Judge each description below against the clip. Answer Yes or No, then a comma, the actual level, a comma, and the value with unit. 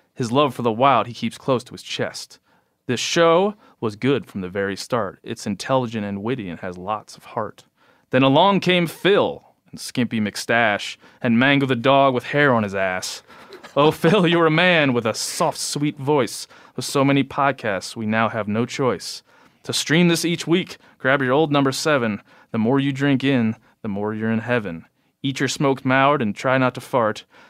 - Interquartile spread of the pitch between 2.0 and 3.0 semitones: No, average, 4.4 semitones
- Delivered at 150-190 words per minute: No, average, 200 wpm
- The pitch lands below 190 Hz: Yes, low, 135 Hz